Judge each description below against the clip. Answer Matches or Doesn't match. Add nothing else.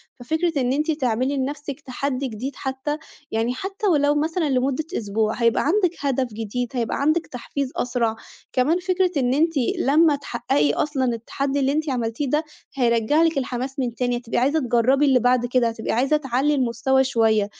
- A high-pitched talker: Matches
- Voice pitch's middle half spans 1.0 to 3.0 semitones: Doesn't match